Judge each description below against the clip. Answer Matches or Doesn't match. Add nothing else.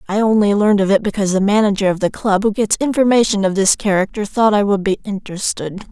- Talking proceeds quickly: Matches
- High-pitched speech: Matches